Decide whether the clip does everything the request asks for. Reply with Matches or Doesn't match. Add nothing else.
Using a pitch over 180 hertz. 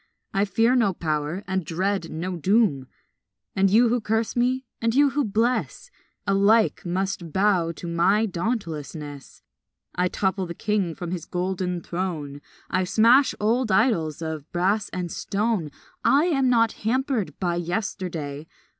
Matches